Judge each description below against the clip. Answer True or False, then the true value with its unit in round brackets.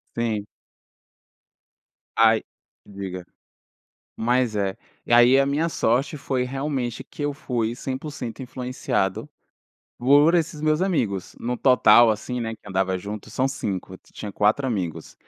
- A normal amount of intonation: True (4.6 semitones)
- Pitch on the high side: False (120 Hz)